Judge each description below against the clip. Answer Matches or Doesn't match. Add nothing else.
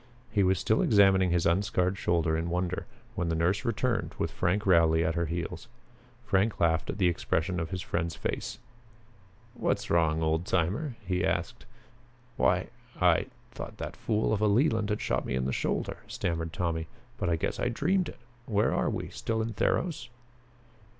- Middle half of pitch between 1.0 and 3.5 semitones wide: Doesn't match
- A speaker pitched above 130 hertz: Doesn't match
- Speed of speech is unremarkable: Matches